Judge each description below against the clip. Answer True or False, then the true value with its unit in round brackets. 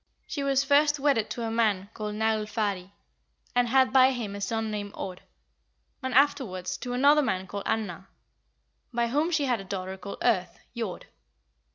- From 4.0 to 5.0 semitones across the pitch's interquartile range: True (4.7 semitones)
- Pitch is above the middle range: True (225 Hz)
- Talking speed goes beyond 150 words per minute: True (170 wpm)